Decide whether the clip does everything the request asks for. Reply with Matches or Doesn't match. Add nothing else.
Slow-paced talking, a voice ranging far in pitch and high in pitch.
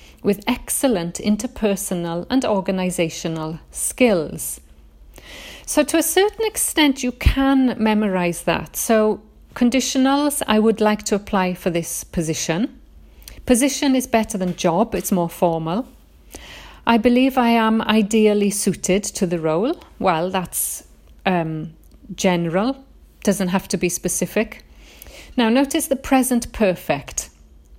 Matches